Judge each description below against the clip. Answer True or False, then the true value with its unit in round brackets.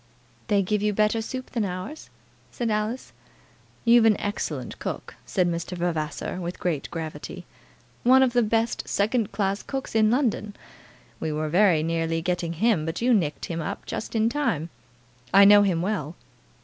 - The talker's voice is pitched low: False (205 Hz)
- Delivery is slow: False (160 wpm)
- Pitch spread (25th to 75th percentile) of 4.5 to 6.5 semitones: True (4.9 semitones)